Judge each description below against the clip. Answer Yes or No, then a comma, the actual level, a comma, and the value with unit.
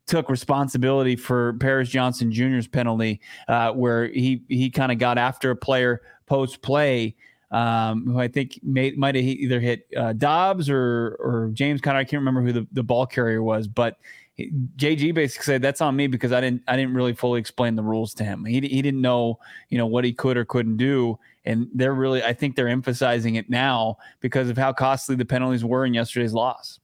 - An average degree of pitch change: No, narrow, 2.0 semitones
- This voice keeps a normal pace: No, fast, 210 wpm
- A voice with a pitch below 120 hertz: No, low, 125 Hz